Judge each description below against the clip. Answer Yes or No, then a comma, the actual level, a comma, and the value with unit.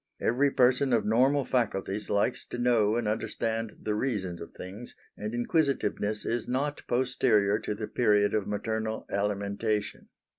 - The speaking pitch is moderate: No, low, 110 Hz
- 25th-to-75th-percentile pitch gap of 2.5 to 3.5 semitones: Yes, average, 3.0 semitones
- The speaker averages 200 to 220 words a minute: No, average, 145 wpm